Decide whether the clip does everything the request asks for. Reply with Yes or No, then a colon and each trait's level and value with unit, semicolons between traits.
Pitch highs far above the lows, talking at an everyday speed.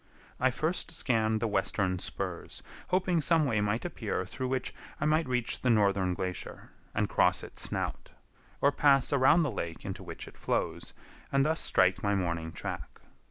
Yes: wide, 6.7 semitones; average, 170 wpm